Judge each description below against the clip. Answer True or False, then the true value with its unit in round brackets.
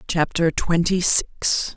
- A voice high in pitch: False (165 Hz)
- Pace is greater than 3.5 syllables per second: False (3.1 syllables/s)